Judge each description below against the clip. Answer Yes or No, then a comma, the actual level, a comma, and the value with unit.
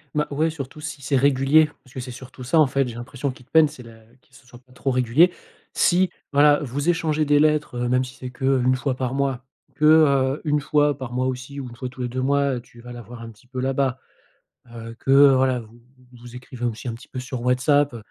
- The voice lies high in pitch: No, low, 130 Hz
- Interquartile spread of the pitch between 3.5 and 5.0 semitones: No, average, 2.7 semitones